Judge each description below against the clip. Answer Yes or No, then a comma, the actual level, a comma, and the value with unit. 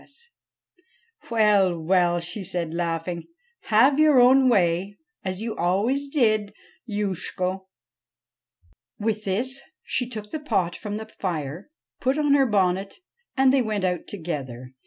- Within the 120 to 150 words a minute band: Yes, average, 140 wpm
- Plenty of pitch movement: Yes, wide, 6.2 semitones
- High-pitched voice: Yes, high, 205 Hz